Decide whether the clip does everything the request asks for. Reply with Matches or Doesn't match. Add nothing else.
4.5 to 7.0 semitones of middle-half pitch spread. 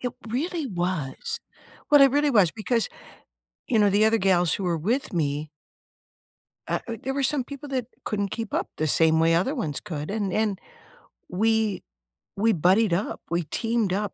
Matches